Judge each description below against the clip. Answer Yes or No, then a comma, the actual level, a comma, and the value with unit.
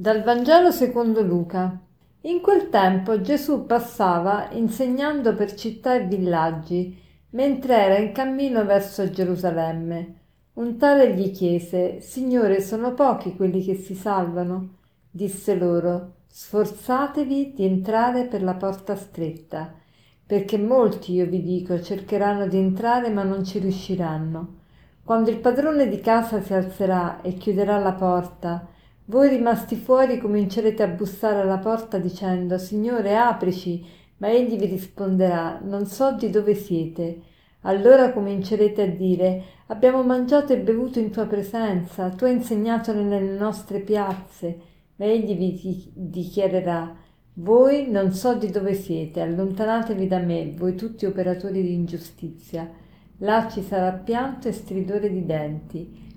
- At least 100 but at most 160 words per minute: Yes, average, 135 wpm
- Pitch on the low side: No, high, 200 Hz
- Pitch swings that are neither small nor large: Yes, average, 3.7 semitones